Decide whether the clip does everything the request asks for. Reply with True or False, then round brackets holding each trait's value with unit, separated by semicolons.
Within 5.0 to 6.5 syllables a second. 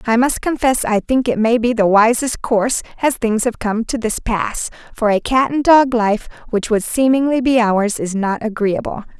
False (4.7 syllables/s)